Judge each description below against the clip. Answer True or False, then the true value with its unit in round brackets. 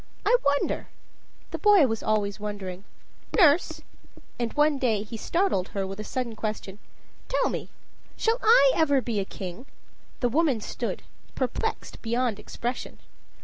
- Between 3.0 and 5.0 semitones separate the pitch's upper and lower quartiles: False (5.4 semitones)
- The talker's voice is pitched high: True (235 Hz)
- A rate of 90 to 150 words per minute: True (145 wpm)